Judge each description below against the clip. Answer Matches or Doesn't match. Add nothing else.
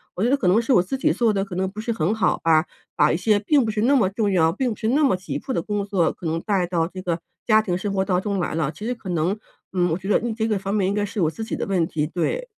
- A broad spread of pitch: Doesn't match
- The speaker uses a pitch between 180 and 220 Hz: Matches